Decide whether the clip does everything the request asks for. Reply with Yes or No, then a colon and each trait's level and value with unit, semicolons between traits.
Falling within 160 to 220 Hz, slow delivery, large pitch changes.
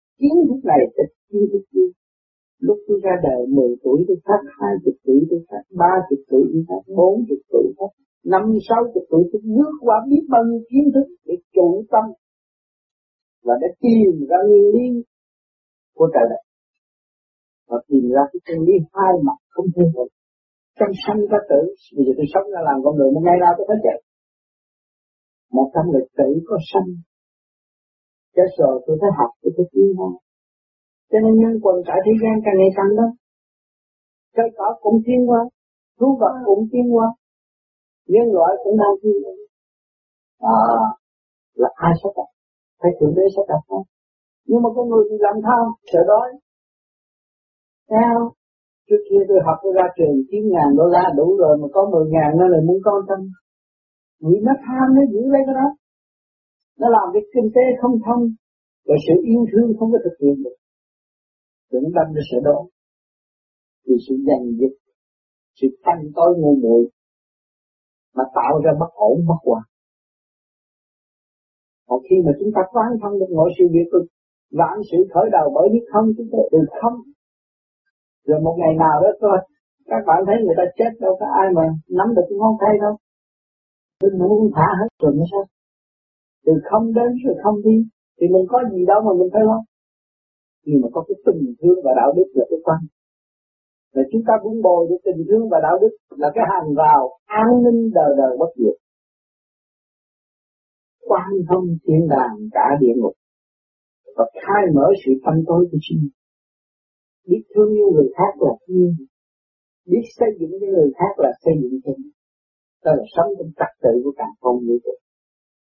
No: high, 190 Hz; average, 180 wpm; wide, 6.5 semitones